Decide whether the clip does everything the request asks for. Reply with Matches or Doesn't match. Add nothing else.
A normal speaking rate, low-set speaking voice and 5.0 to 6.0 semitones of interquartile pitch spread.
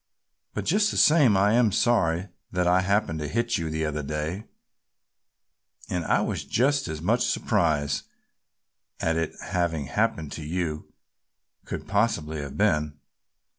Matches